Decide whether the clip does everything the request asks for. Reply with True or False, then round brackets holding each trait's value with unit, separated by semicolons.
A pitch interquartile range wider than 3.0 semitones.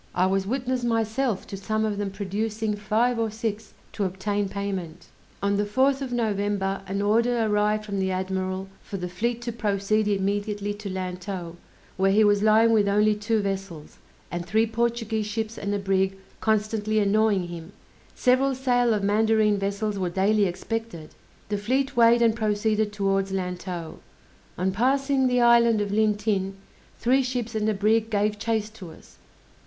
False (2.5 semitones)